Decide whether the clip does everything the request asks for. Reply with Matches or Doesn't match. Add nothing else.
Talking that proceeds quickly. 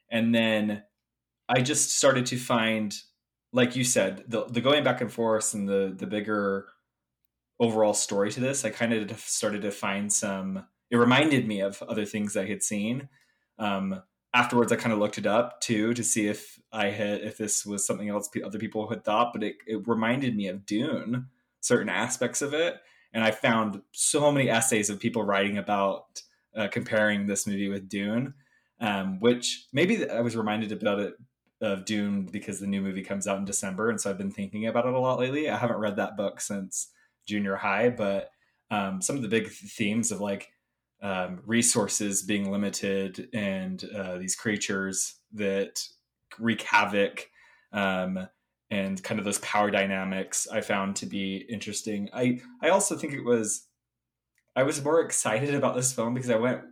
Doesn't match